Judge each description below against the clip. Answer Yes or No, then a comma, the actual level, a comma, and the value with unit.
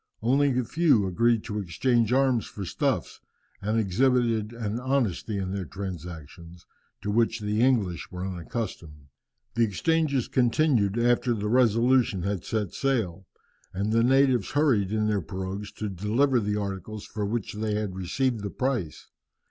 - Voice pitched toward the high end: No, low, 110 Hz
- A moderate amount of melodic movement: Yes, average, 4.1 semitones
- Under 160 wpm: Yes, average, 150 wpm